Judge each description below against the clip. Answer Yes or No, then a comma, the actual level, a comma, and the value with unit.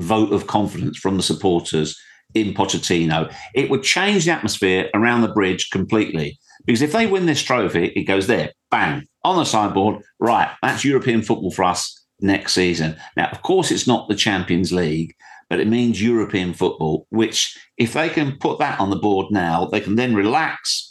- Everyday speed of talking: Yes, average, 185 wpm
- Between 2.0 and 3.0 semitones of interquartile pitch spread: No, average, 4.2 semitones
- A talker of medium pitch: No, low, 100 Hz